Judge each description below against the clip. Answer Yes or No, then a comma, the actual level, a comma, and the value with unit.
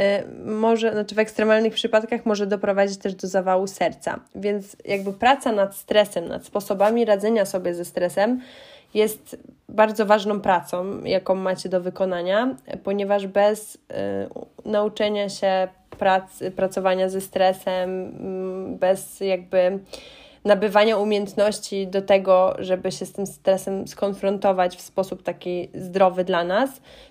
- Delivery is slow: No, average, 125 wpm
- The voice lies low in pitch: No, high, 195 Hz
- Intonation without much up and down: Yes, narrow, 2.0 semitones